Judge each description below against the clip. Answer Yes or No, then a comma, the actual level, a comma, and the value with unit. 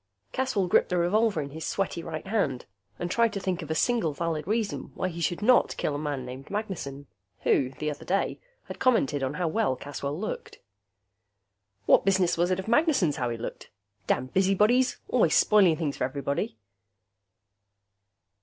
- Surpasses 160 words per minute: Yes, average, 175 wpm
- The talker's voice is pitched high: No, medium, 175 Hz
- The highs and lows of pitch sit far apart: Yes, wide, 6.2 semitones